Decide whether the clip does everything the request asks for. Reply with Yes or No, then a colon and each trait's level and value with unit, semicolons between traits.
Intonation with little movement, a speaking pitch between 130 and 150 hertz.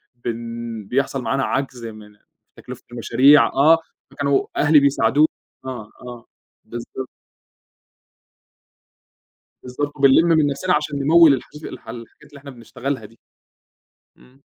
No: average, 3.4 semitones; low, 135 Hz